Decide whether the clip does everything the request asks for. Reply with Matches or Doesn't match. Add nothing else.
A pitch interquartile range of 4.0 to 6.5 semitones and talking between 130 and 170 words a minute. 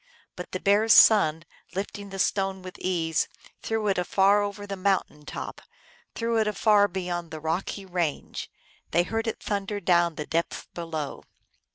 Doesn't match